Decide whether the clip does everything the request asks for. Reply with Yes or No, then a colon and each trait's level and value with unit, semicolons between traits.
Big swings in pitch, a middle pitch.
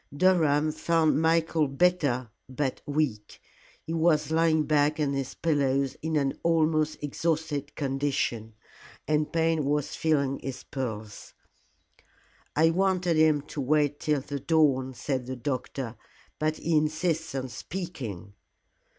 No: average, 2.9 semitones; medium, 150 Hz